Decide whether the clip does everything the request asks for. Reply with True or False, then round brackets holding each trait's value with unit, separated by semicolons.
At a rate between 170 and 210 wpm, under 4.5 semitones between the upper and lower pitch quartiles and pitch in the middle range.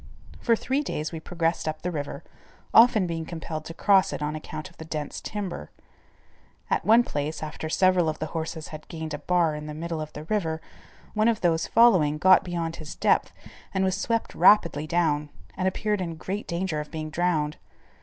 True (195 wpm; 3.3 semitones; 165 Hz)